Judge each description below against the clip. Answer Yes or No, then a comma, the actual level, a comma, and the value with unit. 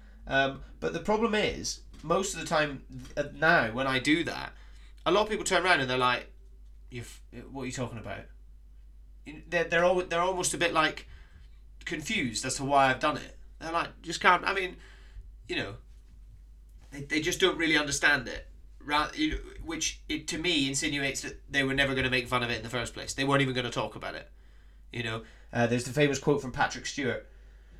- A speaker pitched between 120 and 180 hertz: Yes, low, 135 Hz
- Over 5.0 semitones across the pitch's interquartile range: Yes, wide, 5.6 semitones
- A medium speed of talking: No, fast, 220 wpm